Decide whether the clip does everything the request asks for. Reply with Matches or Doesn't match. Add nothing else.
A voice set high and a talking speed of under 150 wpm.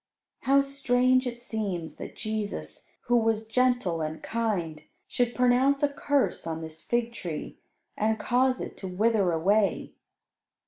Matches